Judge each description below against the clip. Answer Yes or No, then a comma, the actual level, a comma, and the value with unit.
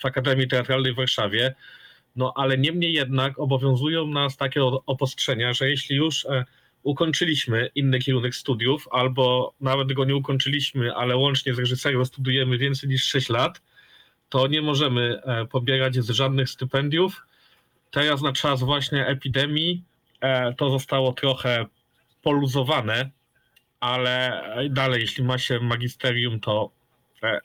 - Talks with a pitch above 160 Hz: No, low, 135 Hz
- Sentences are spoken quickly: No, average, 135 wpm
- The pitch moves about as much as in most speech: No, narrow, 1.6 semitones